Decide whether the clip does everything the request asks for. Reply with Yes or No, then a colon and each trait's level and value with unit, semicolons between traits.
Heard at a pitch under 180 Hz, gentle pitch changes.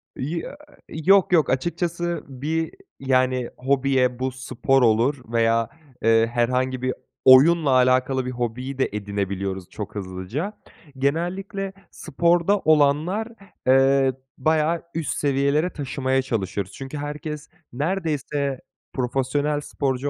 No: low, 135 Hz; average, 3.6 semitones